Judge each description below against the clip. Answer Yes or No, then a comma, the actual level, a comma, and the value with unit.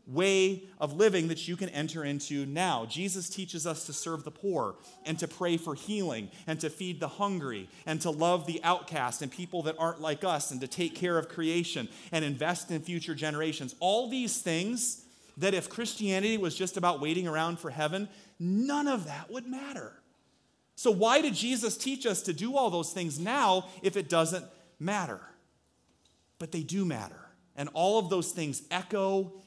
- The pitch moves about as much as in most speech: Yes, average, 3.6 semitones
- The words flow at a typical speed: Yes, average, 185 wpm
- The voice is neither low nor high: Yes, medium, 175 Hz